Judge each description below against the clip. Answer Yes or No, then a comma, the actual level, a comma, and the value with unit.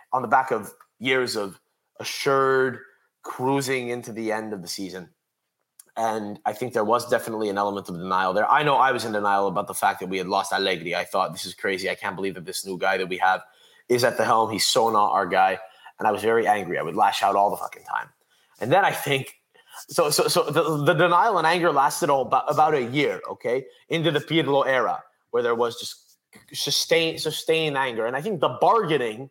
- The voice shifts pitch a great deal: Yes, wide, 7.5 semitones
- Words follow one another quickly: Yes, fast, 225 wpm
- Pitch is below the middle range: Yes, low, 115 Hz